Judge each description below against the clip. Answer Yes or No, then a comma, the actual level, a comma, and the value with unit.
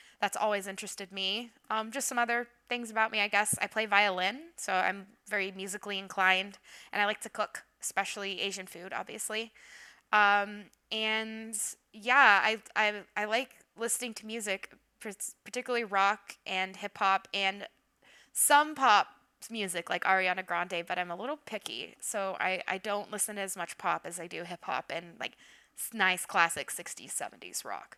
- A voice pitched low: No, high, 205 Hz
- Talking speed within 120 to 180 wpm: Yes, average, 165 wpm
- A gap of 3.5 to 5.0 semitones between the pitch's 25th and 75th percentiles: No, narrow, 2.5 semitones